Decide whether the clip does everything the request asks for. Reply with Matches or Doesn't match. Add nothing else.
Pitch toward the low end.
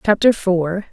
Doesn't match